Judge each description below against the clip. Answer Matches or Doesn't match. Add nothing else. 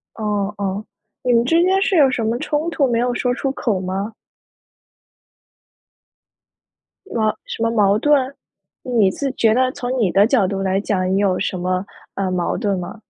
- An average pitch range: Matches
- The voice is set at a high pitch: Matches